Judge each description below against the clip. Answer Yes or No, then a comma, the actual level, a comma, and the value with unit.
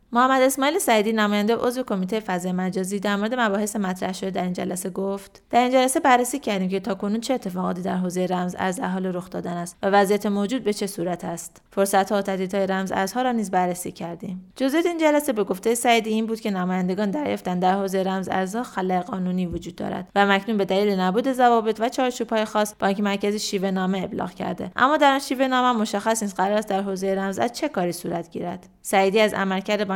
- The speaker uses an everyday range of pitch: Yes, average, 3.3 semitones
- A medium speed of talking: No, fast, 210 wpm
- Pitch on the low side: No, high, 200 Hz